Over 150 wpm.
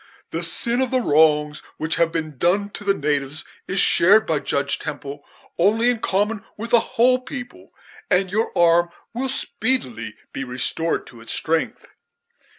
Yes: average, 160 wpm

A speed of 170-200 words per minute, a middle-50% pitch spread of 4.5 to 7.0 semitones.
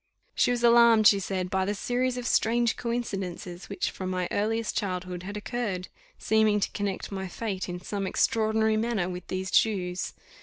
No: average, 175 wpm; average, 3.4 semitones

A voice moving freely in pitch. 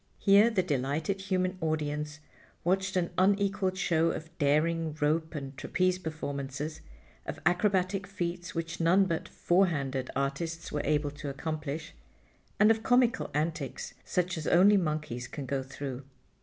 No: average, 4.0 semitones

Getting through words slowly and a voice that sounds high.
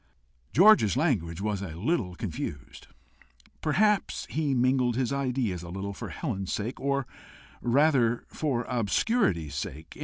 No: slow, 125 wpm; low, 120 Hz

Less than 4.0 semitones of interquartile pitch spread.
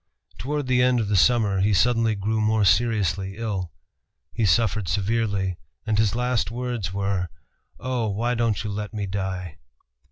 Yes: average, 3.1 semitones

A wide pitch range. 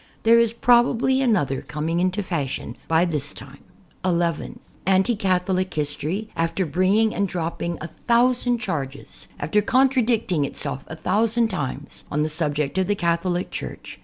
Yes: wide, 6.2 semitones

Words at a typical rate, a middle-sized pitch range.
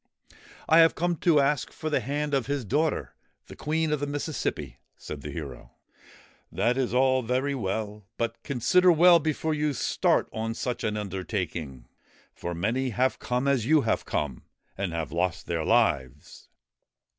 No: average, 170 wpm; wide, 8.0 semitones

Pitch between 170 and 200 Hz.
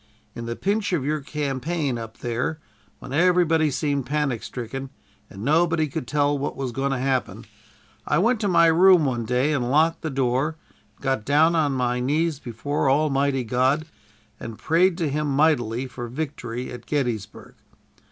No: medium, 140 Hz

